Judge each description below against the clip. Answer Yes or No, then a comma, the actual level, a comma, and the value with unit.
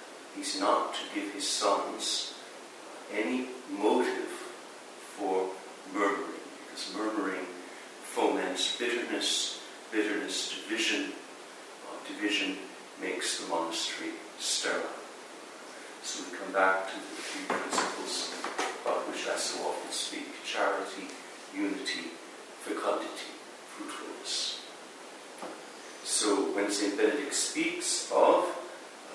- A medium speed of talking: No, slow, 95 wpm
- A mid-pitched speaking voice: No, low, 125 Hz